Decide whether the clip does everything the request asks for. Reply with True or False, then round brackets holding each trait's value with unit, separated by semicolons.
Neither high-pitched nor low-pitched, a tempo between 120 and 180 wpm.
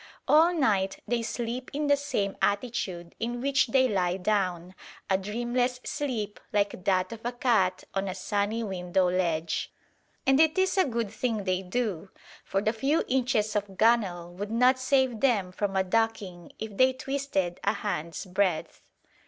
False (215 Hz; 165 wpm)